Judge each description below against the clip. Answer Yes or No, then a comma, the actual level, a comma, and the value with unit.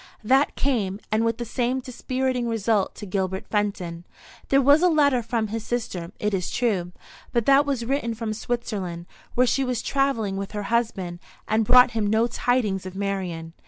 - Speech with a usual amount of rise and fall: Yes, average, 4.2 semitones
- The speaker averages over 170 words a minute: Yes, average, 180 wpm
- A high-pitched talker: Yes, high, 225 Hz